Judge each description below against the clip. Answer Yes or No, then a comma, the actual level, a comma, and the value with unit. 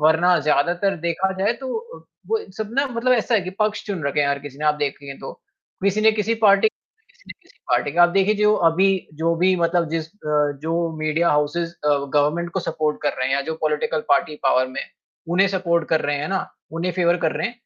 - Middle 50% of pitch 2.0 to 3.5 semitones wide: No, average, 4.4 semitones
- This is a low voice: No, medium, 170 Hz